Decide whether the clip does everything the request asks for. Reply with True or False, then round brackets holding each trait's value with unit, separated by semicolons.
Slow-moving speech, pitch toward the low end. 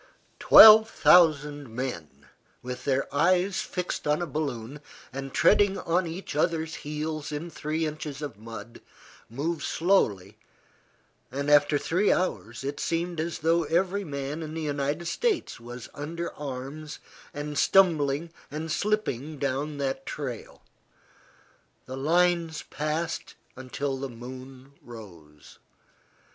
False (125 wpm; 150 Hz)